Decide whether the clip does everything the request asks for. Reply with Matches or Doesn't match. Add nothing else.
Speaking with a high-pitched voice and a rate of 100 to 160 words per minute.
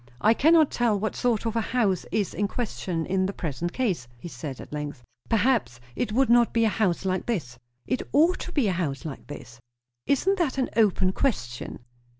Doesn't match